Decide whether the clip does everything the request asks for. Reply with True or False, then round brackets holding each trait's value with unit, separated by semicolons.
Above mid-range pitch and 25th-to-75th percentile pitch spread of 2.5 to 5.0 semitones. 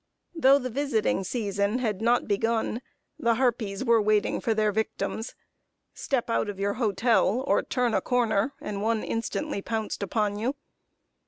True (225 Hz; 2.8 semitones)